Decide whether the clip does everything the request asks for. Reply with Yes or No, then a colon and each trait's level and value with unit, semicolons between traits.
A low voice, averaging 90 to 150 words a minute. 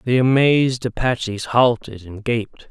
Yes: low, 120 Hz; slow, 135 wpm